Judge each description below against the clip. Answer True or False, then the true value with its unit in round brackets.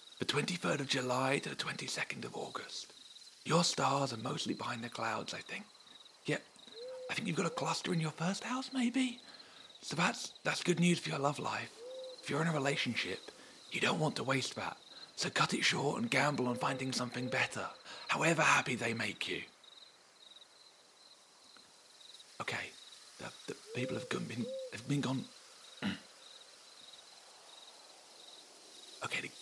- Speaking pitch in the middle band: True (150 Hz)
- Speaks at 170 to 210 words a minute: False (155 wpm)